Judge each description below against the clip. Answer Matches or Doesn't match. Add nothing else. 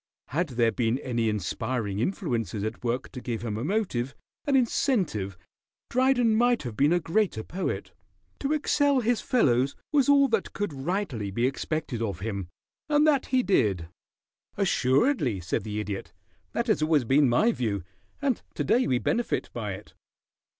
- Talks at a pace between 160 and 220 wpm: Matches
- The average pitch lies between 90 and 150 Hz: Matches